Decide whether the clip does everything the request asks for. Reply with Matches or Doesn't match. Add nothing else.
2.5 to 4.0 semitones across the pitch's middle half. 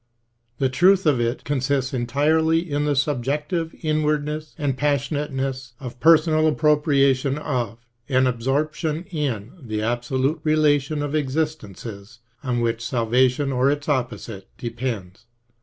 Matches